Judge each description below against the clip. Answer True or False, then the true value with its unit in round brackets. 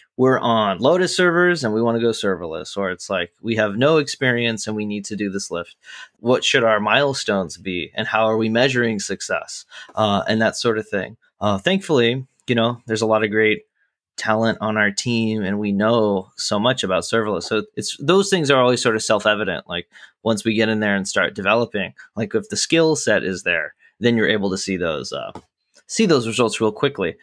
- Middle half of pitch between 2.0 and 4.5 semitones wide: True (2.7 semitones)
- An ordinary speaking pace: False (215 wpm)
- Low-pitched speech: True (110 Hz)